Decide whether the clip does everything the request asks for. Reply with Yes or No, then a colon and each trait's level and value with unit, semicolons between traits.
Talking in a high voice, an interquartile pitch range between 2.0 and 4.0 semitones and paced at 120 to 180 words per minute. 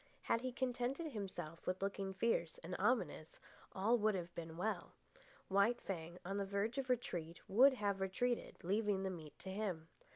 No: high, 195 Hz; average, 4.5 semitones; average, 170 wpm